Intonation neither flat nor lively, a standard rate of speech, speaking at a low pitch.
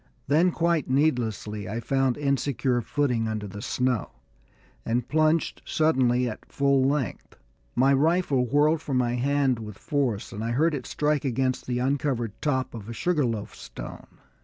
Yes: average, 3.6 semitones; average, 160 wpm; low, 130 Hz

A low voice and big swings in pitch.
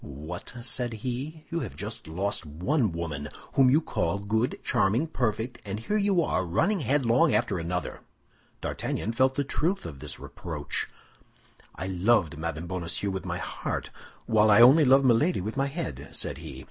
Yes: low, 110 Hz; wide, 7.4 semitones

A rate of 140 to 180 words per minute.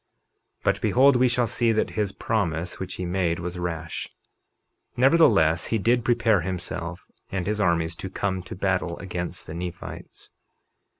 Yes: average, 160 wpm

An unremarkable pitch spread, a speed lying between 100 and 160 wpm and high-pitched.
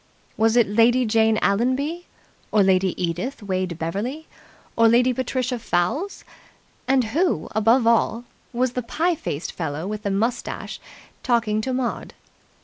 Yes: average, 4.2 semitones; average, 140 wpm; high, 230 Hz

